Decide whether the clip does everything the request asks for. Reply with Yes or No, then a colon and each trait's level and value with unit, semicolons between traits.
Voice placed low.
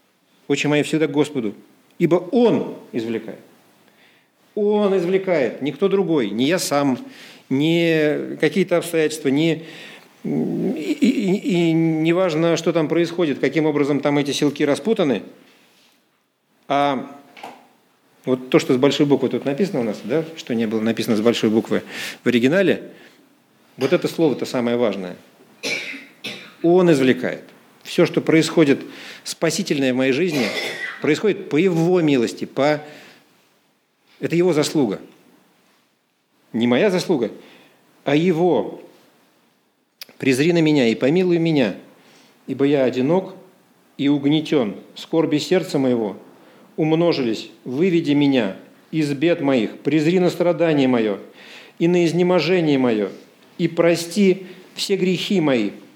No: medium, 160 Hz